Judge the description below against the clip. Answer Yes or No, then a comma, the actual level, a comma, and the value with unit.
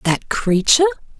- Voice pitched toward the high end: Yes, high, 215 Hz